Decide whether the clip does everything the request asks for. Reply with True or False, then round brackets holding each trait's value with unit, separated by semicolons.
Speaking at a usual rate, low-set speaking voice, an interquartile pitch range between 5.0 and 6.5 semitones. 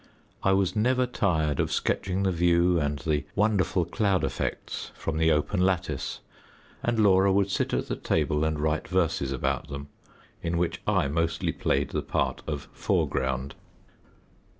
False (155 wpm; 85 Hz; 4.3 semitones)